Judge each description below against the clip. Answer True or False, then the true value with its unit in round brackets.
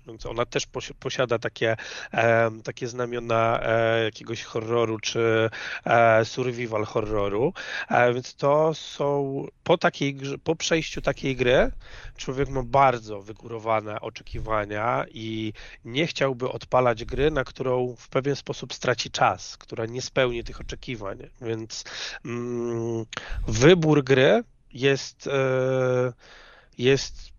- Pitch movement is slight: False (3.1 semitones)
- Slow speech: True (105 wpm)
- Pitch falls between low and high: False (125 Hz)